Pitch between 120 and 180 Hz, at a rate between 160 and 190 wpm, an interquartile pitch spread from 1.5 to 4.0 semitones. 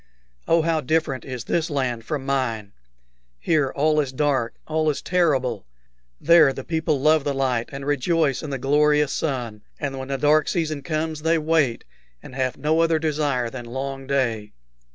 Yes: medium, 140 Hz; average, 175 wpm; average, 3.1 semitones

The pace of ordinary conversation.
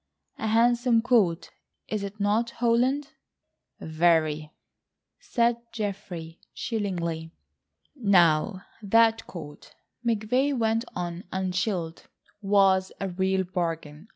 No: slow, 95 wpm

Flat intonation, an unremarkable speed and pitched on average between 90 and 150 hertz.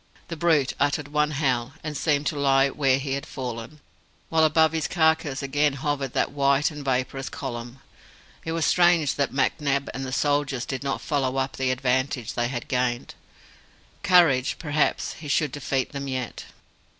Yes: narrow, 2.2 semitones; average, 170 wpm; medium, 140 Hz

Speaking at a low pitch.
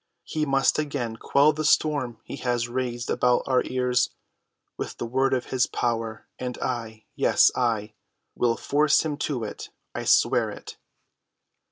Yes: low, 125 Hz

